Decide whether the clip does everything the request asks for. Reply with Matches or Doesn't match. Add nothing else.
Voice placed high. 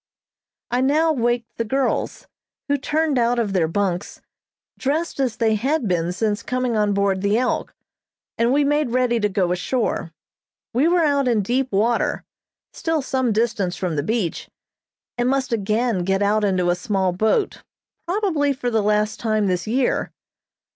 Matches